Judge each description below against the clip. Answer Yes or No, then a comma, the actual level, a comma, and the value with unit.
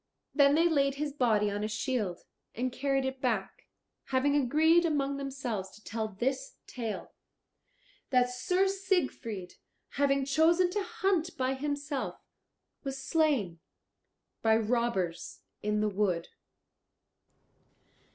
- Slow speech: Yes, slow, 120 wpm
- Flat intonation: No, average, 5.1 semitones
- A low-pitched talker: No, very high, 265 Hz